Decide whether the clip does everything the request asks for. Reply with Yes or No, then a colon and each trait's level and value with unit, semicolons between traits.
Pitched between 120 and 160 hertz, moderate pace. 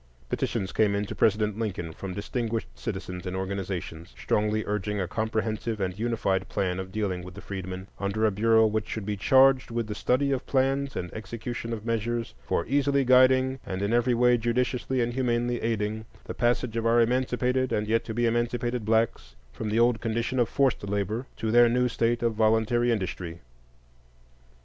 No: low, 110 Hz; average, 185 wpm